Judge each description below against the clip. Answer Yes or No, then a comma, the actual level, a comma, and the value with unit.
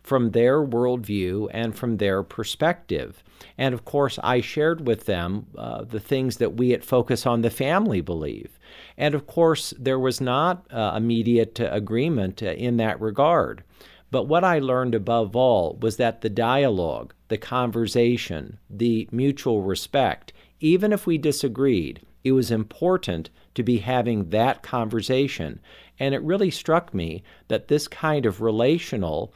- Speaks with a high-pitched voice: No, low, 120 Hz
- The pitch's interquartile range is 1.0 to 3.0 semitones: No, average, 3.7 semitones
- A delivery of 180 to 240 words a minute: No, average, 155 wpm